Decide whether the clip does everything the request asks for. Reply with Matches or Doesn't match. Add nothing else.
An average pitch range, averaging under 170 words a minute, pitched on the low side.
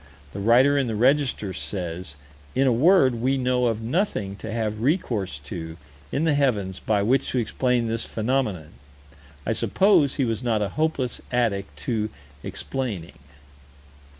Matches